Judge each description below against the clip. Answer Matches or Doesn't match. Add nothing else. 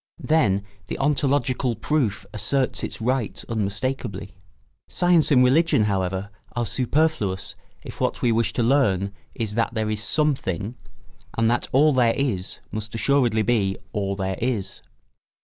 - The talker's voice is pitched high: Doesn't match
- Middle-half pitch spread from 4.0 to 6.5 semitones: Matches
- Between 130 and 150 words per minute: Matches